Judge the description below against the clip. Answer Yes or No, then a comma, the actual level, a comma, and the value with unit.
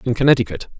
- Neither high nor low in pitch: No, low, 120 Hz